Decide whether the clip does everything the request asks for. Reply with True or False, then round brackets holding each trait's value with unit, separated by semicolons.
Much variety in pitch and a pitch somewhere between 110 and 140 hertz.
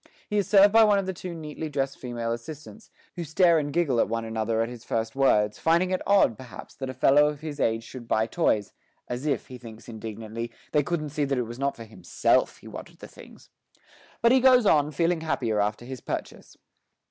True (6.3 semitones; 135 Hz)